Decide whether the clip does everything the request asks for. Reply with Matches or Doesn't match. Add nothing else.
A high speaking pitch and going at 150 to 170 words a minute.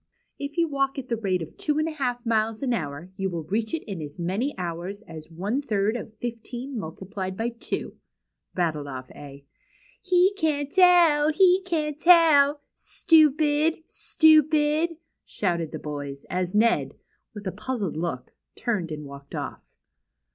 Matches